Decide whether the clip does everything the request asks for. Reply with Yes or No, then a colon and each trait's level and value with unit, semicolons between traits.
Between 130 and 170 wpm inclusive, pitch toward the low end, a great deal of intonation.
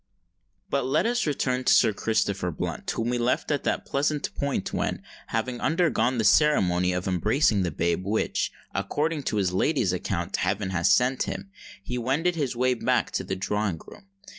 No: average, 180 wpm; low, 120 Hz; wide, 6.8 semitones